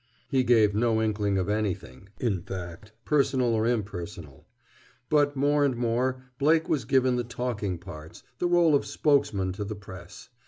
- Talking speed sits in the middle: Yes, average, 160 wpm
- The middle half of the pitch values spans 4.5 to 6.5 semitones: Yes, average, 5.1 semitones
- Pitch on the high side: No, low, 110 Hz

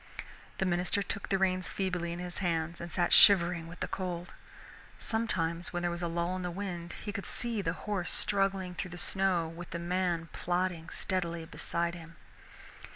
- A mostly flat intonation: Yes, narrow, 1.7 semitones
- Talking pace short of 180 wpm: No, average, 185 wpm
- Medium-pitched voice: Yes, medium, 175 Hz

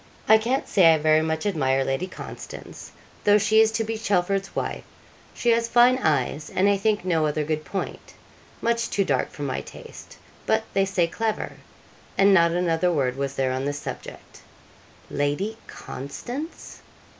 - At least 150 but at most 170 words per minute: Yes, average, 165 wpm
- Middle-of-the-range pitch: Yes, medium, 180 Hz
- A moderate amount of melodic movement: No, wide, 6.5 semitones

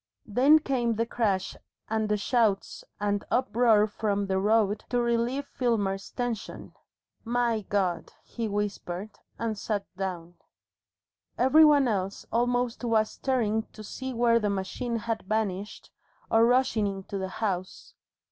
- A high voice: Yes, high, 220 Hz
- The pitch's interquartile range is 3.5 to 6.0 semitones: No, average, 3.1 semitones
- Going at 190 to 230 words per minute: No, slow, 135 wpm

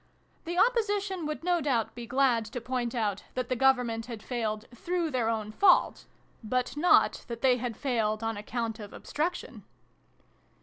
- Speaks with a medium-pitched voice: No, high, 245 Hz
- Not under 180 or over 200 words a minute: No, average, 165 wpm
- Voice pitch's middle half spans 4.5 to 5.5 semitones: Yes, average, 5.0 semitones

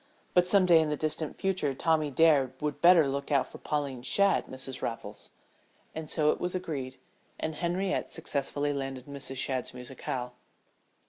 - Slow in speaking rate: No, average, 170 wpm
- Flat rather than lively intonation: No, average, 3.6 semitones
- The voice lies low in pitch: No, medium, 145 Hz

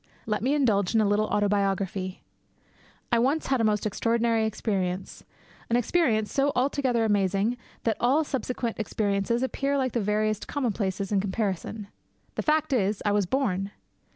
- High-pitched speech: Yes, high, 215 Hz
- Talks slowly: No, average, 155 wpm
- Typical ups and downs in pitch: Yes, average, 3.8 semitones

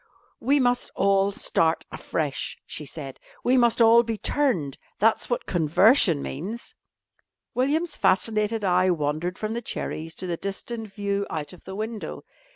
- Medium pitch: No, high, 200 Hz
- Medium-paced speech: Yes, average, 150 wpm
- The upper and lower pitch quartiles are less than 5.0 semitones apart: No, wide, 5.6 semitones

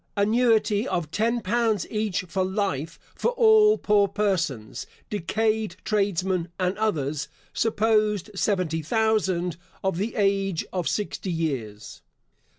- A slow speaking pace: Yes, slow, 115 wpm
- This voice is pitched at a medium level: No, high, 200 Hz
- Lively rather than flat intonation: No, average, 4.0 semitones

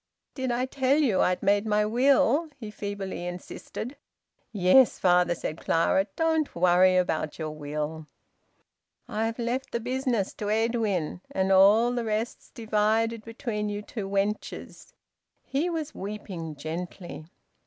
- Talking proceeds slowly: Yes, slow, 130 wpm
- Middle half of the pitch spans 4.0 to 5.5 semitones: Yes, average, 4.7 semitones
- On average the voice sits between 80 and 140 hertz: No, high, 210 Hz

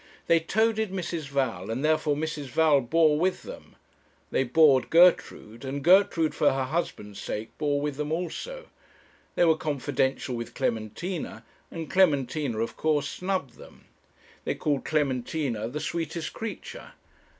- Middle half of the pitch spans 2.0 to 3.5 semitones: No, average, 4.1 semitones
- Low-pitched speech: No, medium, 150 Hz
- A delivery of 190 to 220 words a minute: No, average, 140 wpm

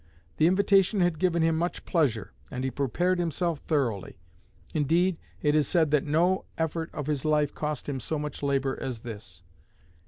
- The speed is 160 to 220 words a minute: Yes, average, 175 wpm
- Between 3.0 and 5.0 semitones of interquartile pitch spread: Yes, average, 3.8 semitones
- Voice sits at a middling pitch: Yes, medium, 150 Hz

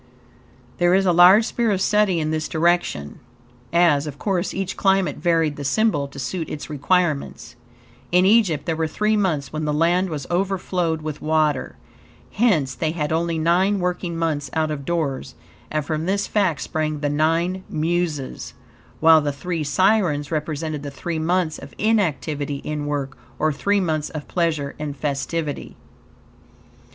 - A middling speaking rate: Yes, average, 160 wpm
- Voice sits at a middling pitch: Yes, medium, 160 Hz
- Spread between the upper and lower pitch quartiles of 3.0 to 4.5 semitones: Yes, average, 3.3 semitones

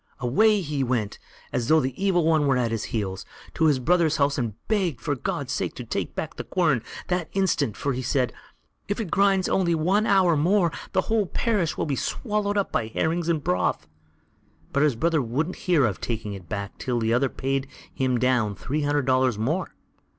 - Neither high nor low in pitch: Yes, medium, 145 Hz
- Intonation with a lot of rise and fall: Yes, wide, 6.4 semitones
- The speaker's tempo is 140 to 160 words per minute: No, fast, 205 wpm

